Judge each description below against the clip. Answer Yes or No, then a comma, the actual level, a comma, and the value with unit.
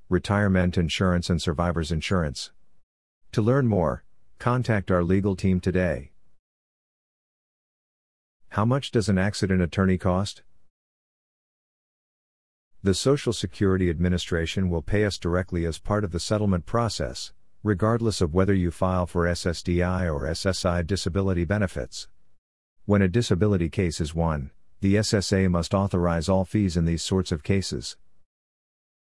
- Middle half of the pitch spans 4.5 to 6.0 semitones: No, average, 2.8 semitones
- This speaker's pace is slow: Yes, slow, 130 wpm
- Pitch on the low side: Yes, very low, 90 Hz